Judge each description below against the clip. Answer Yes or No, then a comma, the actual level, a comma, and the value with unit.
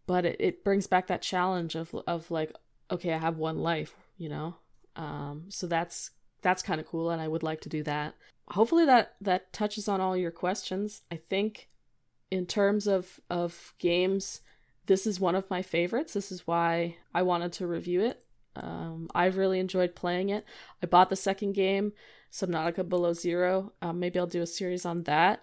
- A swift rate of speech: No, average, 195 wpm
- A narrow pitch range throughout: Yes, narrow, 2.3 semitones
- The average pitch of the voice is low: No, medium, 180 Hz